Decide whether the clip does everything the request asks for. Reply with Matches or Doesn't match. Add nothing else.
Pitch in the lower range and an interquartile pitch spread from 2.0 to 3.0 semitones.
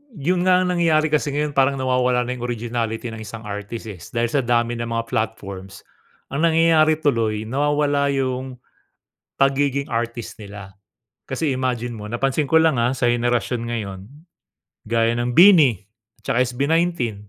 Doesn't match